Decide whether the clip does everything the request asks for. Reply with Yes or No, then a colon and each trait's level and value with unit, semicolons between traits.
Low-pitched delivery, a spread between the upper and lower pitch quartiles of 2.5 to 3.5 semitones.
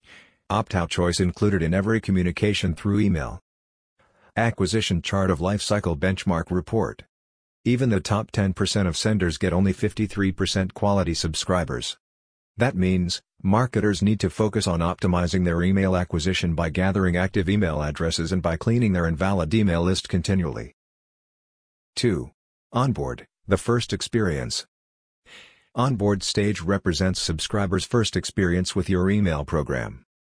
Yes: very low, 95 Hz; average, 3.0 semitones